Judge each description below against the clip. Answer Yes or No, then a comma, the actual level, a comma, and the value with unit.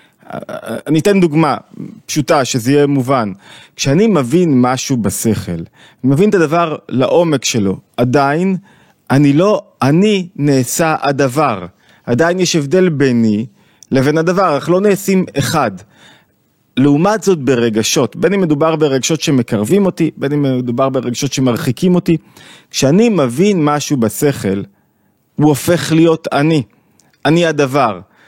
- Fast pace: No, average, 125 wpm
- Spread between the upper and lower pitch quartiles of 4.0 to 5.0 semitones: Yes, average, 4.7 semitones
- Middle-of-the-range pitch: Yes, medium, 145 Hz